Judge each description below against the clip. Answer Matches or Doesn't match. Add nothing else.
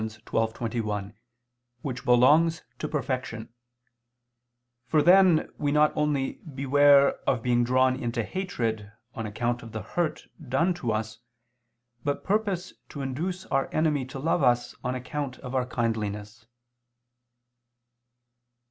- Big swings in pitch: Doesn't match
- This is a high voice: Doesn't match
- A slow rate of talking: Matches